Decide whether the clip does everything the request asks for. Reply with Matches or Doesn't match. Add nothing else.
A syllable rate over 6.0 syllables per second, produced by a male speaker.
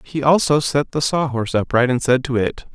Doesn't match